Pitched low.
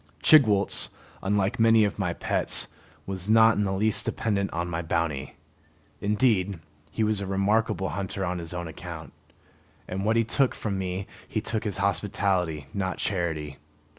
Yes: low, 100 Hz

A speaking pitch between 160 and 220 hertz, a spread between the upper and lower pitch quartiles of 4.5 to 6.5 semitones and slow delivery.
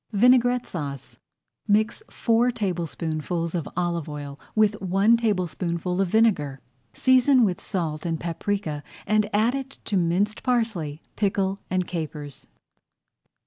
Yes: medium, 185 Hz; average, 4.8 semitones; slow, 120 wpm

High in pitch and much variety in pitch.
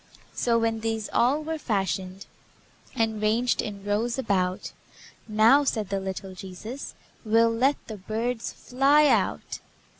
No: high, 225 Hz; average, 3.5 semitones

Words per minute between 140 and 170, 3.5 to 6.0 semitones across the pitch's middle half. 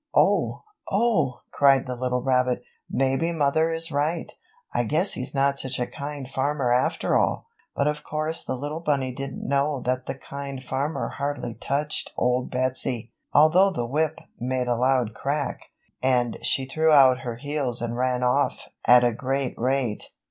No: average, 165 wpm; average, 2.8 semitones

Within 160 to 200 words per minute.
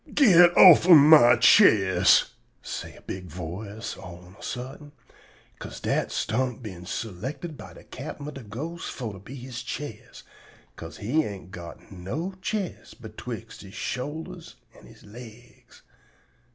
No: average, 150 wpm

